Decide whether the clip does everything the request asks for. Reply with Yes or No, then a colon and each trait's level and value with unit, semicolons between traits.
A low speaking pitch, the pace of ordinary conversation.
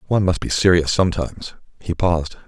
Yes: very low, 85 Hz; average, 170 wpm